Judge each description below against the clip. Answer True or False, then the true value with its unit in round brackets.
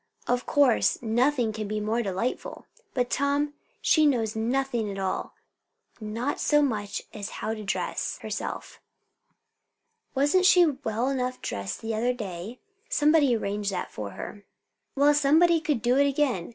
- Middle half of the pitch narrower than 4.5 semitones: False (4.9 semitones)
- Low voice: False (245 Hz)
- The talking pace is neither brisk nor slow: True (150 wpm)